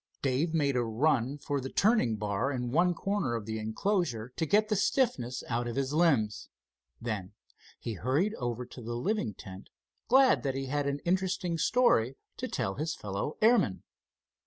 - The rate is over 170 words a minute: Yes, average, 180 wpm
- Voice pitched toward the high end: No, low, 135 Hz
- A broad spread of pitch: Yes, wide, 7.1 semitones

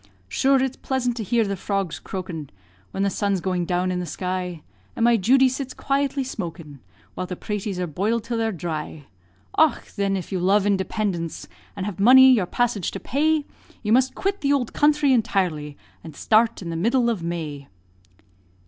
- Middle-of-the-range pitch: No, high, 200 Hz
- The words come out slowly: No, average, 185 wpm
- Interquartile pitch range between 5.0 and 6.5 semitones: Yes, wide, 5.6 semitones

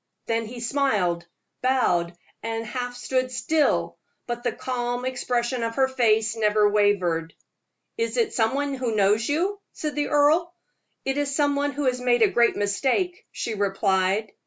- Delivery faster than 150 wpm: Yes, average, 160 wpm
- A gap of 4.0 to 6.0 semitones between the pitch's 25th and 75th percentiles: Yes, average, 4.5 semitones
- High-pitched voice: Yes, high, 245 Hz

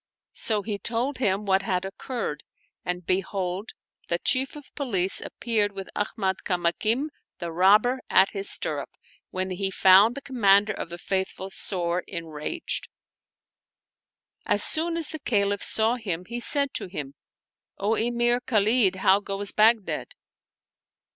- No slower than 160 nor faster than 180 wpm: No, average, 145 wpm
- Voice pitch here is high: Yes, high, 200 Hz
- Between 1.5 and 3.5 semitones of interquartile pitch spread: No, average, 4.0 semitones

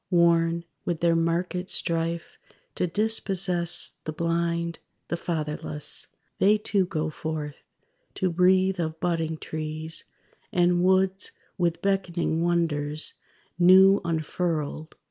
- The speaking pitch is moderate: Yes, medium, 170 Hz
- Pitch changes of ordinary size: No, narrow, 2.1 semitones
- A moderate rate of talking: No, slow, 105 wpm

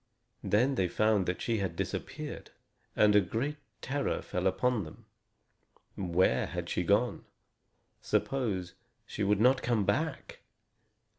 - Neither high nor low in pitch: No, low, 105 Hz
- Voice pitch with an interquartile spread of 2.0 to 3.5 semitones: No, average, 5.1 semitones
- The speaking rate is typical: No, slow, 130 wpm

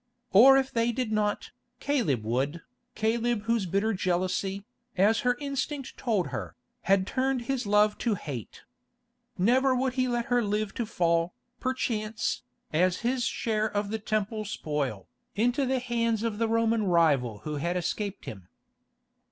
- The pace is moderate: Yes, average, 150 wpm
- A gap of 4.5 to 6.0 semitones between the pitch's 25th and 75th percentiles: Yes, average, 4.8 semitones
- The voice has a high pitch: Yes, high, 215 Hz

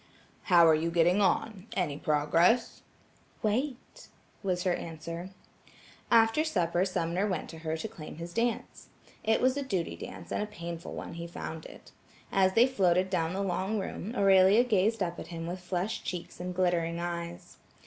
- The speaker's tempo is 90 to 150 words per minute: No, average, 170 wpm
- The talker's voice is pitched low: No, medium, 180 Hz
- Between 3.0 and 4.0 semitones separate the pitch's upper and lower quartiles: Yes, average, 3.6 semitones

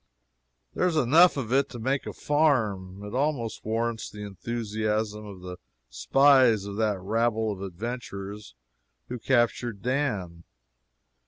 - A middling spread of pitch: Yes, average, 4.0 semitones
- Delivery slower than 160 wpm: Yes, slow, 135 wpm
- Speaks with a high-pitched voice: No, low, 110 Hz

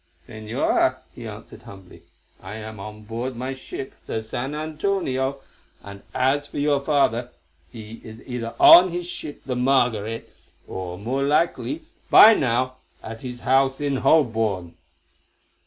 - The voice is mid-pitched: No, low, 125 Hz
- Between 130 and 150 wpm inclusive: Yes, average, 140 wpm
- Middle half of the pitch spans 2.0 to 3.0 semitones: No, average, 4.1 semitones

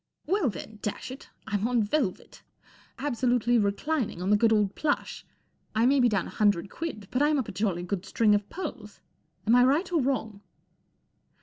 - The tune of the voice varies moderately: Yes, average, 4.7 semitones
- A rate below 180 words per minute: No, average, 190 wpm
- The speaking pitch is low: No, high, 225 Hz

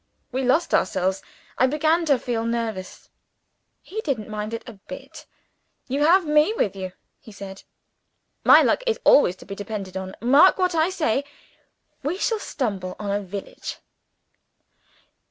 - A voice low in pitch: No, high, 235 Hz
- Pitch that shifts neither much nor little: No, wide, 7.6 semitones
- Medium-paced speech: Yes, average, 155 wpm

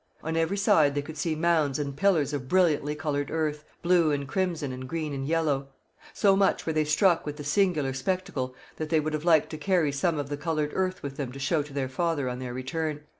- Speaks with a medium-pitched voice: Yes, medium, 150 Hz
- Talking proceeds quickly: Yes, fast, 230 wpm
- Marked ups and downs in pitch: No, average, 2.8 semitones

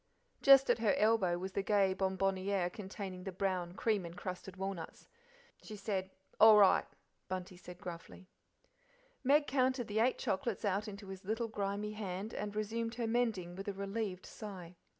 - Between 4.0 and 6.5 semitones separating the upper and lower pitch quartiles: No, average, 2.7 semitones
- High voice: Yes, high, 200 Hz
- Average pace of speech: Yes, average, 160 wpm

